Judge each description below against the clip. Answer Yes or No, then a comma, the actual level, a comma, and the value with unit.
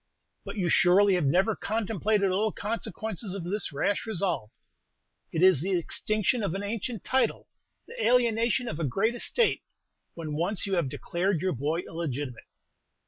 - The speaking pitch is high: Yes, high, 195 Hz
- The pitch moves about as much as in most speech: Yes, average, 4.4 semitones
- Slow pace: No, average, 160 wpm